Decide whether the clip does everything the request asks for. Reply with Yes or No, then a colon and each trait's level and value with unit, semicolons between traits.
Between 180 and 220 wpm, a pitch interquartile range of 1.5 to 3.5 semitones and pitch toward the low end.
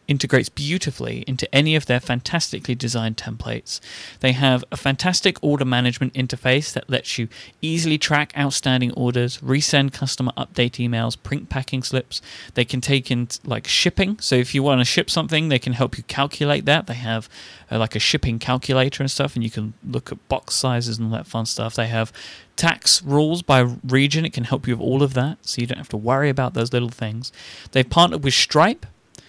Yes: average, 200 wpm; average, 2.8 semitones; low, 130 Hz